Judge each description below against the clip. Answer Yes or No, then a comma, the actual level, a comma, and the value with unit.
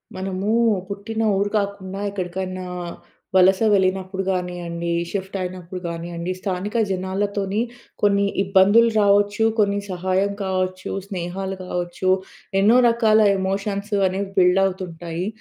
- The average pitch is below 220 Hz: Yes, high, 190 Hz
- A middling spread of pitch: No, narrow, 1.5 semitones